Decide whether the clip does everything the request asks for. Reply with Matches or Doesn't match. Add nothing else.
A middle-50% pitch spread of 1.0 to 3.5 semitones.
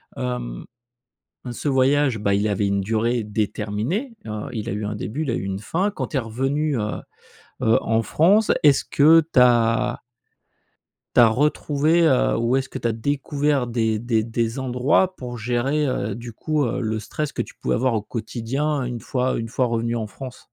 Doesn't match